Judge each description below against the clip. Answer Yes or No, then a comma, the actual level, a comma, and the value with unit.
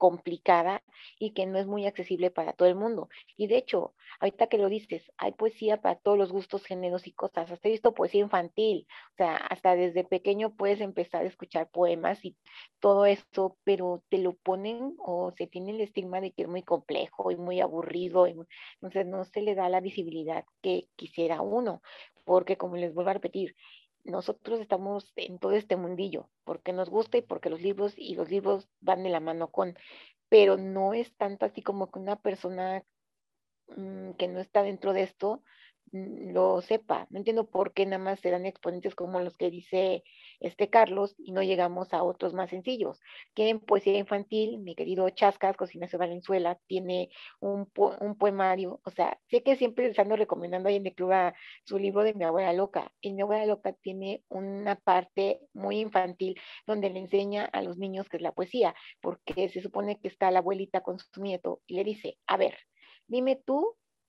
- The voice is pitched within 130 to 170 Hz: No, high, 190 Hz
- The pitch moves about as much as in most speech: No, narrow, 2.0 semitones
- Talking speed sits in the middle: No, fast, 195 wpm